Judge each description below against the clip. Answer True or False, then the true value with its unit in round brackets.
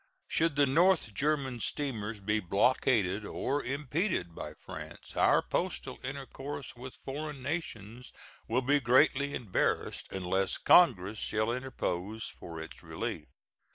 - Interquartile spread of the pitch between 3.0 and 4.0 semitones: False (5.2 semitones)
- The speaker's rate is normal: False (120 wpm)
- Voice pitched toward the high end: False (125 Hz)